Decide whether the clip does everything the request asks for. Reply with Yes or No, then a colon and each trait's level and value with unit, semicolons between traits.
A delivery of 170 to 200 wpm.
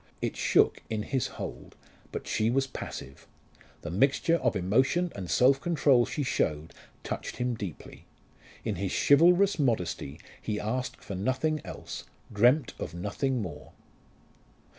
No: average, 140 wpm